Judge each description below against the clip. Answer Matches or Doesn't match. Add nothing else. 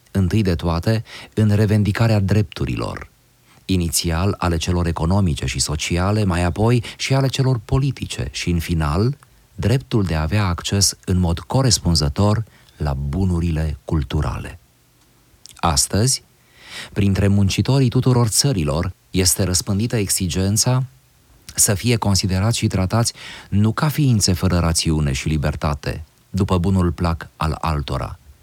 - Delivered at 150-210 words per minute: Doesn't match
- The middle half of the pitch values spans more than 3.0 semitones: Matches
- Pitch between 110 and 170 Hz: Doesn't match